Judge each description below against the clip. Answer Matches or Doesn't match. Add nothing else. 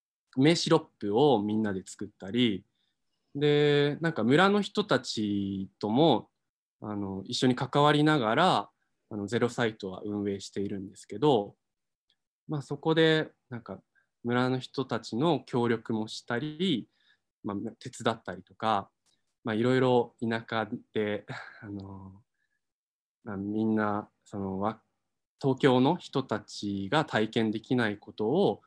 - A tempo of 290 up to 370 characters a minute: Doesn't match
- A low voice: Matches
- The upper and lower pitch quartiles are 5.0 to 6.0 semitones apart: Doesn't match